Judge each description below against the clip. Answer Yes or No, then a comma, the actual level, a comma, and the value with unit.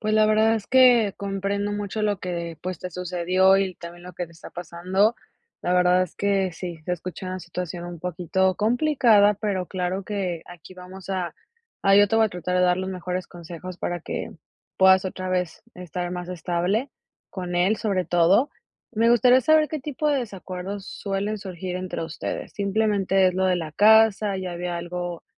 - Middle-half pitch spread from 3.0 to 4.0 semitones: No, narrow, 2.5 semitones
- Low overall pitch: No, medium, 185 Hz